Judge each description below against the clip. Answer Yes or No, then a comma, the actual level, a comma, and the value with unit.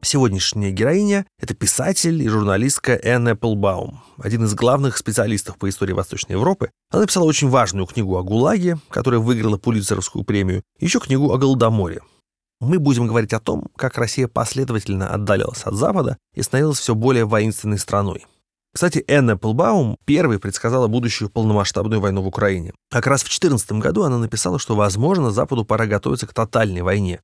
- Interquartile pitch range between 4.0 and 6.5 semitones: Yes, average, 4.5 semitones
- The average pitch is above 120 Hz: No, low, 115 Hz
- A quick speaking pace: Yes, fast, 165 wpm